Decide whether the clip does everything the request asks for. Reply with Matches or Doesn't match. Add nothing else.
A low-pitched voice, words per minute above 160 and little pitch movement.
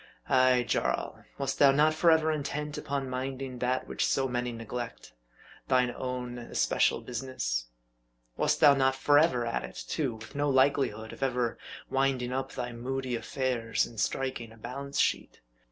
Doesn't match